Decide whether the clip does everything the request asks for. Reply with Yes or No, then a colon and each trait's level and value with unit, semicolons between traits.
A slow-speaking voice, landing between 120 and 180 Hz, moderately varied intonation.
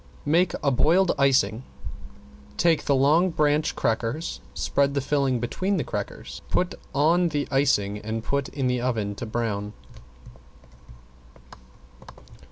Yes: slow, 125 wpm; medium, 140 Hz; average, 4.7 semitones